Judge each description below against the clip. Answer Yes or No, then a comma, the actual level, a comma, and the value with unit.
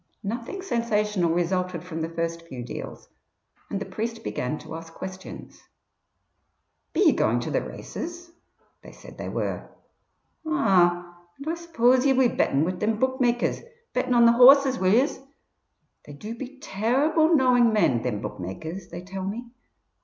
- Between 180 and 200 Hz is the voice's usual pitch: No, high, 215 Hz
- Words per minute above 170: No, average, 155 wpm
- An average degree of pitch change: No, wide, 6.5 semitones